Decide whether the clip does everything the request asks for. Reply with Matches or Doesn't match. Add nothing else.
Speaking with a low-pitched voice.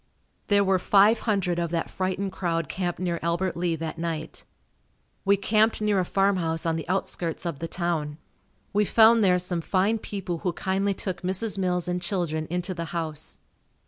Doesn't match